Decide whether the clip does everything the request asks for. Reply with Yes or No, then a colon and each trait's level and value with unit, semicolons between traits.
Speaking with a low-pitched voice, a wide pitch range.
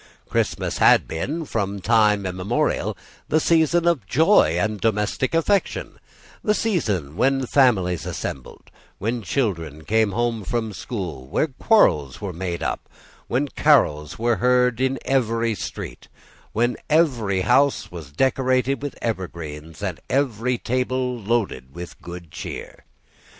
Yes: low, 115 Hz; wide, 6.4 semitones